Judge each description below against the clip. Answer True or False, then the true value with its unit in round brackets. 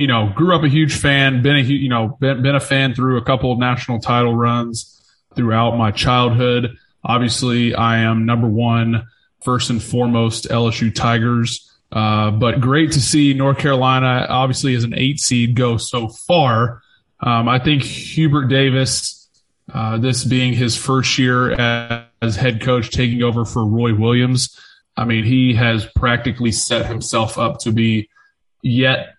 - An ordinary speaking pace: True (165 wpm)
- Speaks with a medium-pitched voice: False (120 Hz)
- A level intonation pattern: True (2.0 semitones)